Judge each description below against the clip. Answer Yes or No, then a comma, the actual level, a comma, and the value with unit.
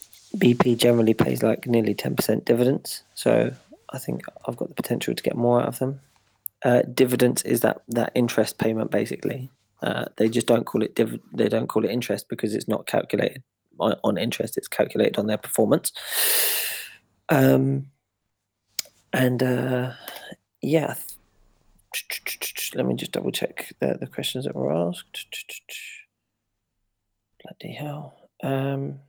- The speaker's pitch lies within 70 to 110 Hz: No, low, 125 Hz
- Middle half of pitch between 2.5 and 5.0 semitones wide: Yes, average, 3.1 semitones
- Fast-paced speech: No, average, 145 wpm